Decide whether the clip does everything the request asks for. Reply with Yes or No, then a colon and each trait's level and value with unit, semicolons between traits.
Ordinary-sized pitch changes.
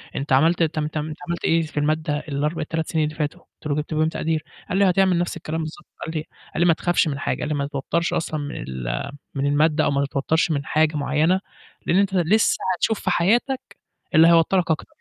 No: narrow, 2.3 semitones